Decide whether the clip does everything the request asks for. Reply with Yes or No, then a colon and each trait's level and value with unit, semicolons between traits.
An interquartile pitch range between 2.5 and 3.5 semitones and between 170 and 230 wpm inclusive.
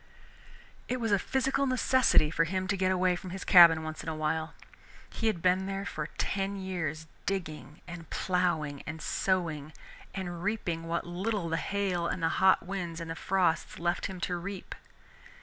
Yes: average, 3.0 semitones; average, 180 wpm